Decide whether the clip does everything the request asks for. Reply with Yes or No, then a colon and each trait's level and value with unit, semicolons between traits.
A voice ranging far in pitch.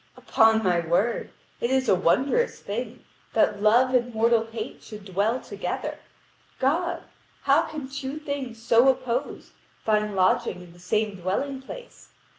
No: average, 4.0 semitones